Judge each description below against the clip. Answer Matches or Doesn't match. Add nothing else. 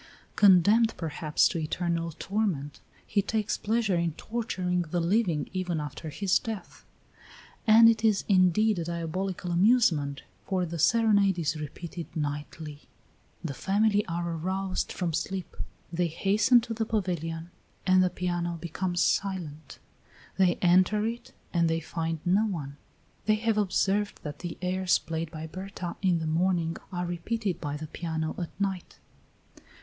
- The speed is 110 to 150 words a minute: Matches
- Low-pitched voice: Doesn't match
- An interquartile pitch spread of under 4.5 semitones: Matches